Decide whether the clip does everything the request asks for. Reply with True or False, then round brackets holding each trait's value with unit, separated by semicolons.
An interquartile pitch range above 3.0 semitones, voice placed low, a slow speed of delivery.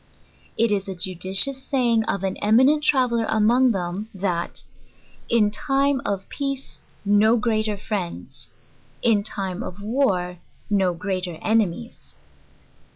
False (4.0 semitones; 210 Hz; 115 wpm)